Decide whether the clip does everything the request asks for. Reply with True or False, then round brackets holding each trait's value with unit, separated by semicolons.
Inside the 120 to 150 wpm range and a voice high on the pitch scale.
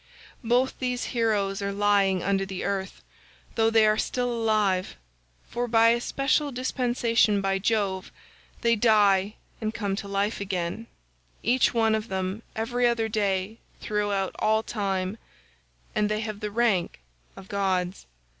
True (145 wpm; 210 Hz)